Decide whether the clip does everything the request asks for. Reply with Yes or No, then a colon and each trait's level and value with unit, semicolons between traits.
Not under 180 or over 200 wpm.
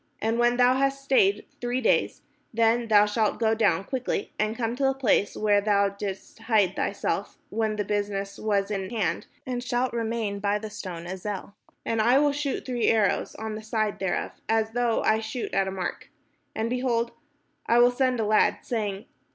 Yes: average, 190 wpm